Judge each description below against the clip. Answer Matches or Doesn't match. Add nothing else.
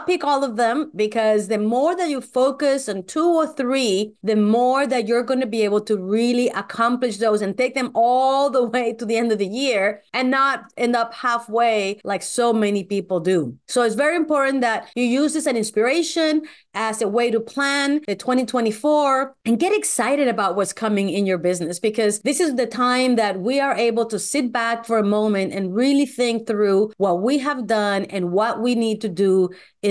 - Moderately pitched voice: Doesn't match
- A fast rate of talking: Matches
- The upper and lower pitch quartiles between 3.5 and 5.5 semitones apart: Matches